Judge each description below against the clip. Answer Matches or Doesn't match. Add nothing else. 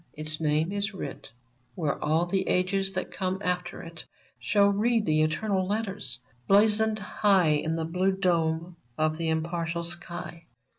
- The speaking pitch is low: Doesn't match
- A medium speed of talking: Matches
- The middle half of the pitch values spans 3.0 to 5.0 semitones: Matches